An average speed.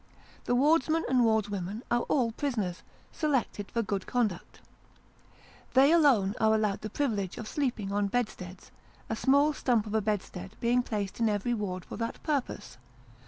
Yes: average, 150 wpm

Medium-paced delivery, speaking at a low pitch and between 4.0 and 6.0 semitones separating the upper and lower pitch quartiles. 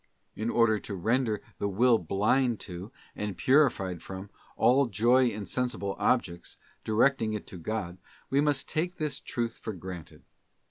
Yes: average, 150 wpm; low, 110 Hz; average, 4.7 semitones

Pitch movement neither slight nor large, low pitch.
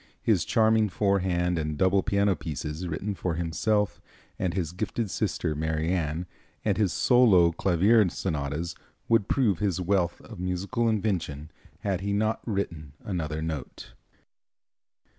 Yes: average, 4.1 semitones; very low, 90 Hz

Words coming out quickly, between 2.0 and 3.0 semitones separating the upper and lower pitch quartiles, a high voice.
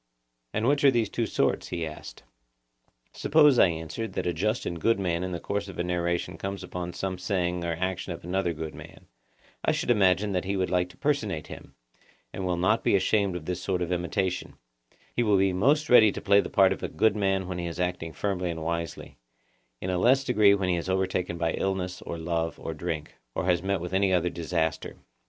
No: fast, 220 wpm; narrow, 2.5 semitones; very low, 90 Hz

